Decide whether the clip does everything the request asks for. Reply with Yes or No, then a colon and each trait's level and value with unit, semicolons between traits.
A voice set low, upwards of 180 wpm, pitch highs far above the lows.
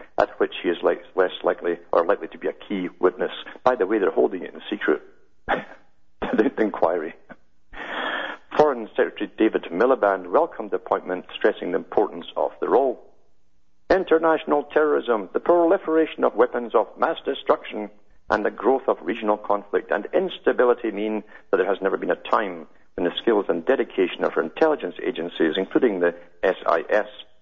No: low, 105 Hz; average, 160 wpm; wide, 6.0 semitones